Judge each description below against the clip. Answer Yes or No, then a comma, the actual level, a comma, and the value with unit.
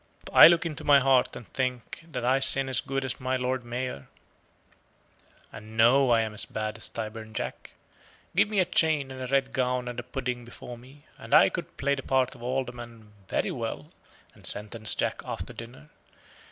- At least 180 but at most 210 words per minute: Yes, average, 190 wpm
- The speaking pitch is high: No, low, 125 Hz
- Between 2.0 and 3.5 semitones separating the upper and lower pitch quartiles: Yes, narrow, 2.4 semitones